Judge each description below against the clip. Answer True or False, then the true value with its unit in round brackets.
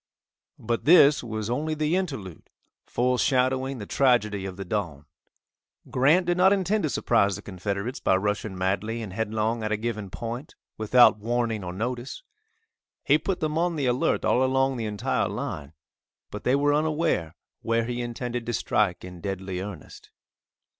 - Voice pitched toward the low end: True (115 Hz)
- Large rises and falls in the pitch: False (4.9 semitones)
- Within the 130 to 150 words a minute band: False (160 wpm)